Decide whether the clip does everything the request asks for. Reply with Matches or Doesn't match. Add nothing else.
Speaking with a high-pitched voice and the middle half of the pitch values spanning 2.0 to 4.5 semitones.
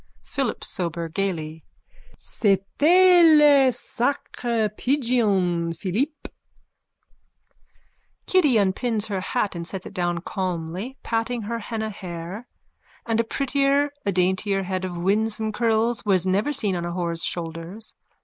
Doesn't match